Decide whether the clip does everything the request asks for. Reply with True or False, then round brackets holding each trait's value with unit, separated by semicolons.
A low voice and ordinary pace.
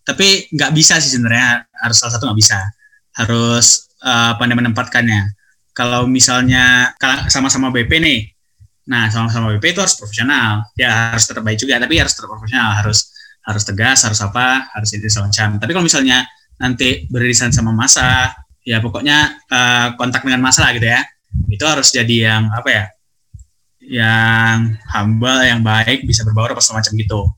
False (120 Hz; 160 wpm)